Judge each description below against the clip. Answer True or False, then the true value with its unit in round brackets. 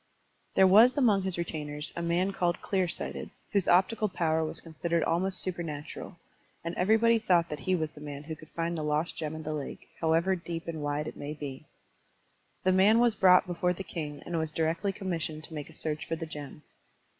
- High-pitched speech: False (170 Hz)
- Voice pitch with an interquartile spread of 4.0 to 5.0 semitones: False (3.3 semitones)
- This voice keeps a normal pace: False (210 wpm)